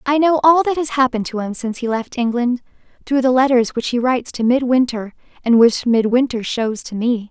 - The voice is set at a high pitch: Yes, high, 245 Hz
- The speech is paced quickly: Yes, fast, 215 wpm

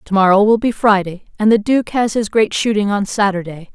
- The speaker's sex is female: Yes, female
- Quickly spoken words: Yes, fast, 225 wpm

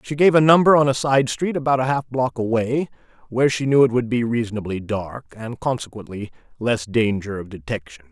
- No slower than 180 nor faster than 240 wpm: Yes, average, 200 wpm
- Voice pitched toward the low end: Yes, low, 120 Hz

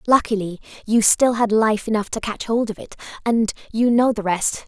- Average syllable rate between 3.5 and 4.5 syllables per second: No, 5.1 syllables/s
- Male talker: No, female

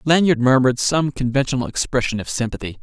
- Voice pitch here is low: Yes, low, 130 Hz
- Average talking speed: Yes, average, 150 wpm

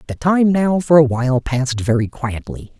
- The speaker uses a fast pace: No, average, 195 wpm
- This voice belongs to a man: Yes, male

